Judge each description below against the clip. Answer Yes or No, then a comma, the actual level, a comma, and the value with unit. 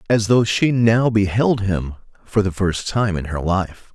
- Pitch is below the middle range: Yes, low, 100 Hz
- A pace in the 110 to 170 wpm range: No, average, 200 wpm